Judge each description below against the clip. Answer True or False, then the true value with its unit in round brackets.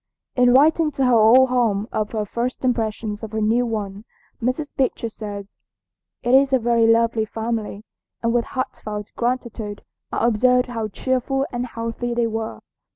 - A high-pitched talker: True (230 Hz)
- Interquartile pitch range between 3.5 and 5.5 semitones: False (2.4 semitones)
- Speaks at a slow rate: False (160 wpm)